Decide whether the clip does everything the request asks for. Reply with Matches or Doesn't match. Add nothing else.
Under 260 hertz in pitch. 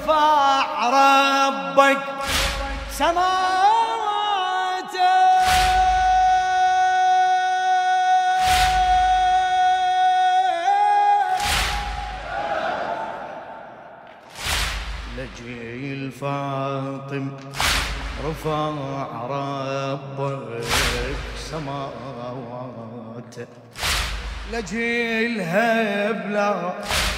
Doesn't match